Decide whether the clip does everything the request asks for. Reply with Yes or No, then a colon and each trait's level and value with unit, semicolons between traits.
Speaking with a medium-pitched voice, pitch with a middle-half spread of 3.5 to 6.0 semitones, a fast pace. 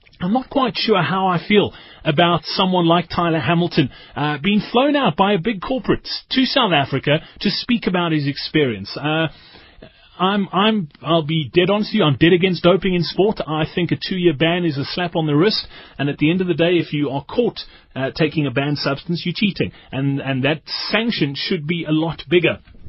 Yes: medium, 170 Hz; average, 4.2 semitones; fast, 215 wpm